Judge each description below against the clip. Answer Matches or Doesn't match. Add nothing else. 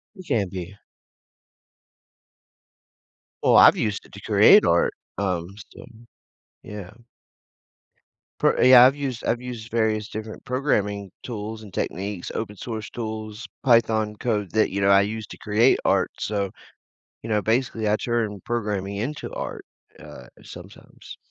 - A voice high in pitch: Doesn't match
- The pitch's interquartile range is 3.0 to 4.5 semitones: Doesn't match